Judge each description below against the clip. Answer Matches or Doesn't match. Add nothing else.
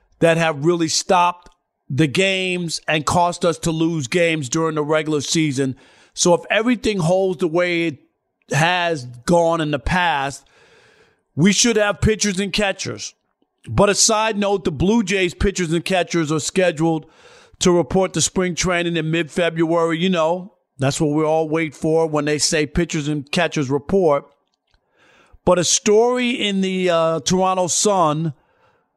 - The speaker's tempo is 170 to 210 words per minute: Doesn't match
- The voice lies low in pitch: Doesn't match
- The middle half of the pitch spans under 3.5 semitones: Matches